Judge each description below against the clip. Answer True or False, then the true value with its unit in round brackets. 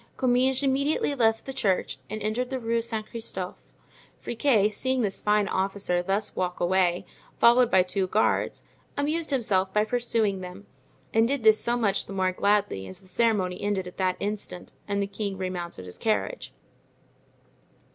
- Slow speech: False (165 wpm)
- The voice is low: False (210 Hz)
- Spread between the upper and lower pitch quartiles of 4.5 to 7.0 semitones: False (3.9 semitones)